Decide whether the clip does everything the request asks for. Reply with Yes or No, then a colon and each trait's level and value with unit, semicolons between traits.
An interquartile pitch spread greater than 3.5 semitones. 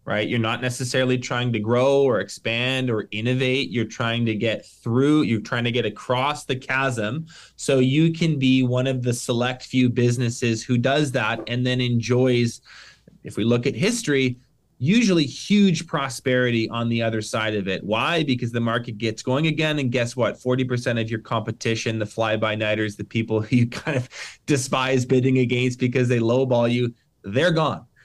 No: narrow, 2.4 semitones